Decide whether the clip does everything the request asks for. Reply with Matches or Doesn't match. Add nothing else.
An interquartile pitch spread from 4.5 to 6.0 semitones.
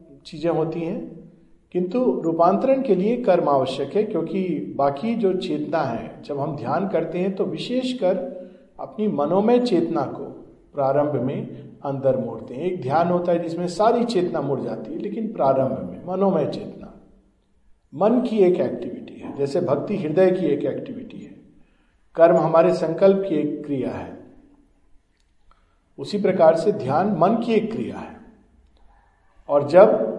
Matches